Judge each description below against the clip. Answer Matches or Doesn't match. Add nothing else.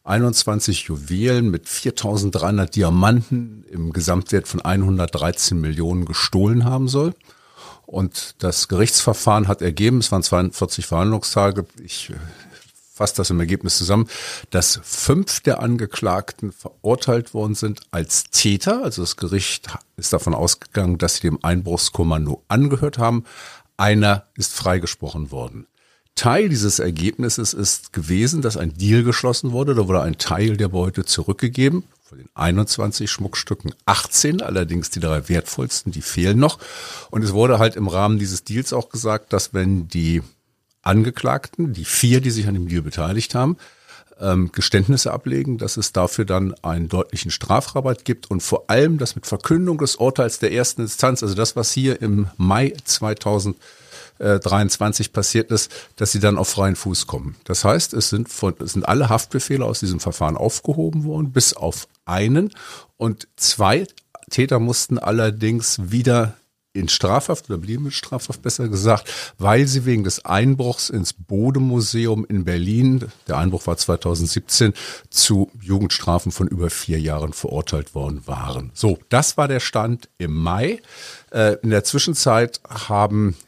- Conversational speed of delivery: Matches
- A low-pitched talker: Matches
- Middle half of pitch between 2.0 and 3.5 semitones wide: Doesn't match